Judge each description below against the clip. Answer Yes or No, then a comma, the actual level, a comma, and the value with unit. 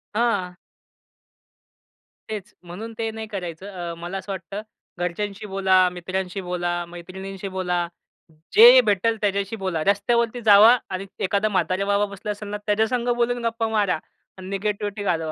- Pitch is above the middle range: Yes, high, 200 Hz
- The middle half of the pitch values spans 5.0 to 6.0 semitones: No, average, 2.8 semitones